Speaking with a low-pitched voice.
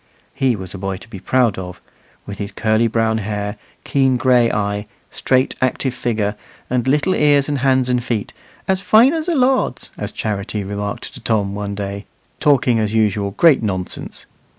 Yes: low, 115 Hz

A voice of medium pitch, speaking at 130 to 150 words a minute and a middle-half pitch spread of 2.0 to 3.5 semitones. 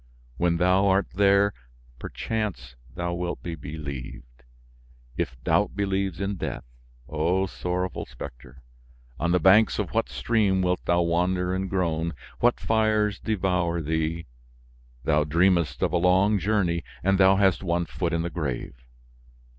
No: very low, 90 Hz; average, 140 wpm; average, 2.7 semitones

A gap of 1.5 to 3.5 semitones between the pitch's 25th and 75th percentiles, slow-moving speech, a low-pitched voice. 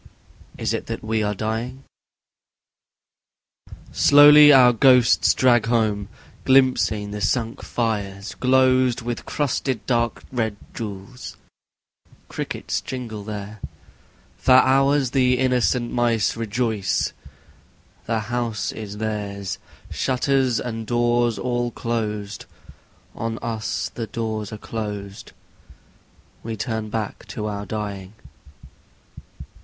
Yes: average, 2.9 semitones; slow, 105 wpm; low, 115 Hz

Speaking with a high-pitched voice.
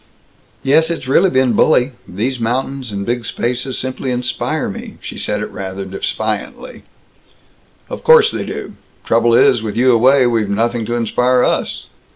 No: low, 125 Hz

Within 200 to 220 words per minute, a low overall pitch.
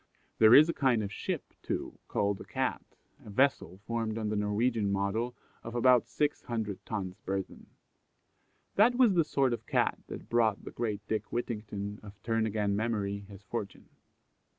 No: average, 165 wpm; low, 110 Hz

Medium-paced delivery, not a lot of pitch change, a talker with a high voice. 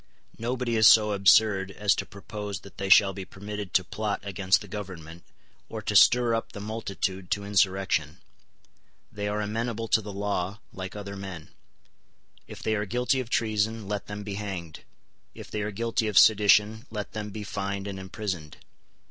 No: average, 175 wpm; narrow, 1.9 semitones; low, 105 Hz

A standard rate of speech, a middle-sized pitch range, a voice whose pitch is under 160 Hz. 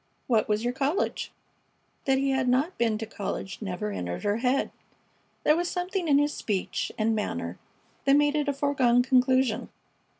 No: average, 170 wpm; average, 4.7 semitones; very high, 255 Hz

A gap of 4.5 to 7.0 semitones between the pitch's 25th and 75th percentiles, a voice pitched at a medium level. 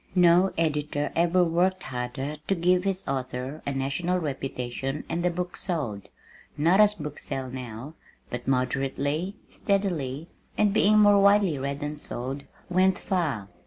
Yes: average, 5.2 semitones; medium, 150 Hz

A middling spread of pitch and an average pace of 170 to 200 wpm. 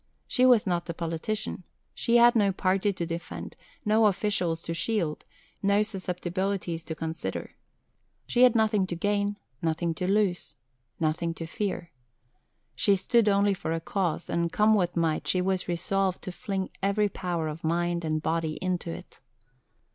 No: average, 3.5 semitones; average, 160 wpm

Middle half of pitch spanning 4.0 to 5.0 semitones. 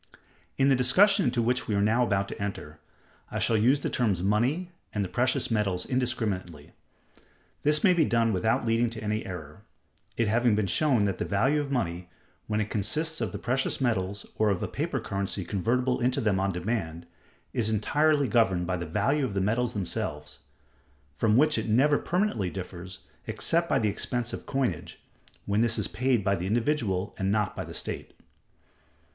Yes: average, 4.6 semitones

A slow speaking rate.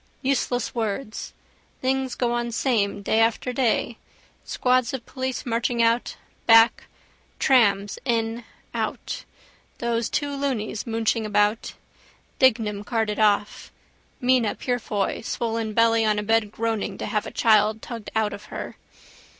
Yes: slow, 130 wpm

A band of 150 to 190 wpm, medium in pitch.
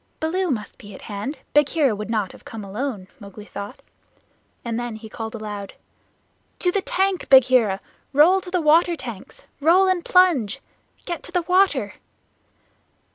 No: average, 155 wpm; very high, 265 Hz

